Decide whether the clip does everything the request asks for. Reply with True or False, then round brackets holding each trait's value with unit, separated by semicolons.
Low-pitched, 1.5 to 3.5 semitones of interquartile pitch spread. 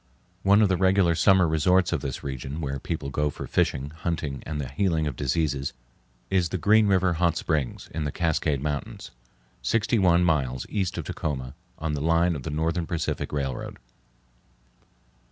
False (80 Hz; 3.9 semitones)